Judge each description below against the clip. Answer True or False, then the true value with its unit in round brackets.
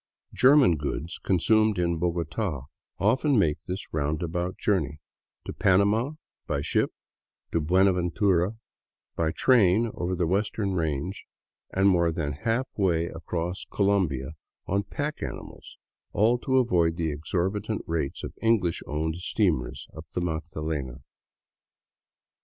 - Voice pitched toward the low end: True (90 Hz)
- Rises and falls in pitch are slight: False (4.1 semitones)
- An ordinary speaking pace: False (125 wpm)